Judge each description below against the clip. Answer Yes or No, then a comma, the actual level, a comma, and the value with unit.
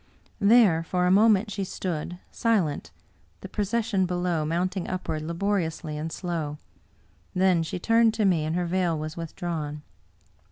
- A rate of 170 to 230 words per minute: No, average, 150 wpm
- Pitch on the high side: No, medium, 180 Hz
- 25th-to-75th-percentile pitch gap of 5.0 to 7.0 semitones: No, average, 3.6 semitones